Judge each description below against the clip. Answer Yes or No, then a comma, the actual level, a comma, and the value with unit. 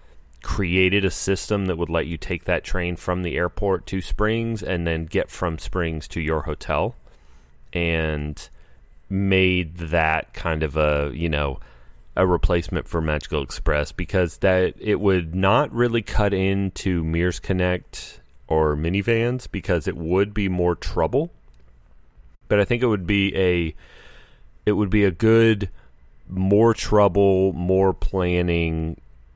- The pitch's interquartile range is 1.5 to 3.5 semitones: No, average, 3.9 semitones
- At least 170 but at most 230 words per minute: No, average, 145 wpm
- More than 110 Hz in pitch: No, very low, 90 Hz